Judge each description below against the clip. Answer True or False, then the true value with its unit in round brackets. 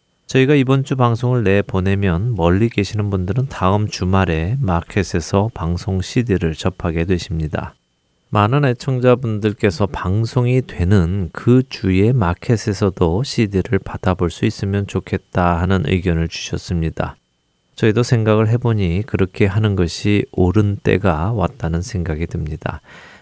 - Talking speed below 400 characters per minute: True (300 characters per minute)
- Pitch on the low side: True (100 Hz)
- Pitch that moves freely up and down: False (4.4 semitones)